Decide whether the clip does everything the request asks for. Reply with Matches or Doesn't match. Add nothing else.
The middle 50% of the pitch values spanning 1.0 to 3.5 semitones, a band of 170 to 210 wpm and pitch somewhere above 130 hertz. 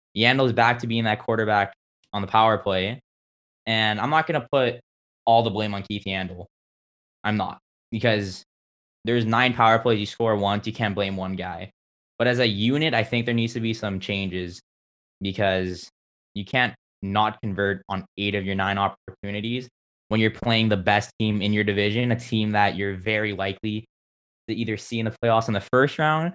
Doesn't match